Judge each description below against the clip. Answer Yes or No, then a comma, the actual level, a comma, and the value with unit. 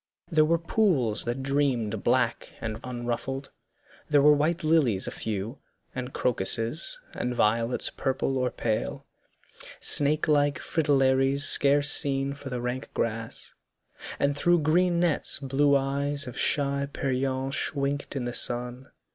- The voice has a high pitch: No, low, 135 Hz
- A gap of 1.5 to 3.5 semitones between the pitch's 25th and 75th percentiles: Yes, average, 2.8 semitones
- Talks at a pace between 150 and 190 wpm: No, slow, 135 wpm